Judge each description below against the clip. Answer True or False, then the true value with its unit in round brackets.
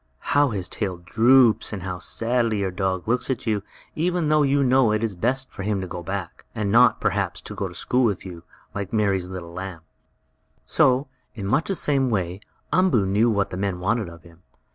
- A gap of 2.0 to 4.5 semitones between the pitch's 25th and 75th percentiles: False (5.1 semitones)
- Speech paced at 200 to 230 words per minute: True (205 wpm)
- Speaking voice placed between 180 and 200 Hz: False (105 Hz)